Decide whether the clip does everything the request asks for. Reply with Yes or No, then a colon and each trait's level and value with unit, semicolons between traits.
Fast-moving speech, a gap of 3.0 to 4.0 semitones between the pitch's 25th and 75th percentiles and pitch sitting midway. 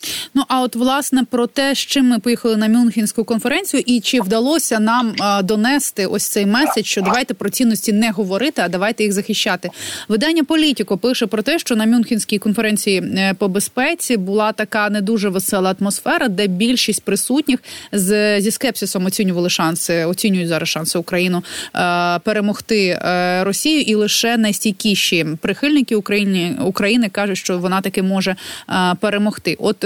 No: fast, 160 wpm; average, 3.5 semitones; high, 215 Hz